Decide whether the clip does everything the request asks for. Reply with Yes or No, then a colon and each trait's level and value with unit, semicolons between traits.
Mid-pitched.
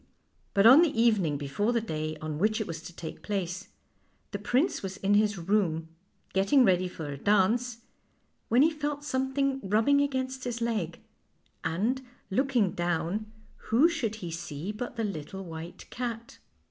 No: high, 210 Hz